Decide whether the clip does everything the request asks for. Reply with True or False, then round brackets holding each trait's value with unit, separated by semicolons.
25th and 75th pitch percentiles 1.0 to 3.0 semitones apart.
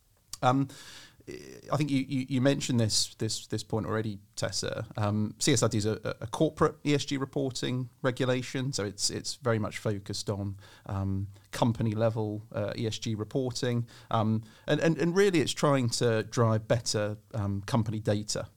False (3.7 semitones)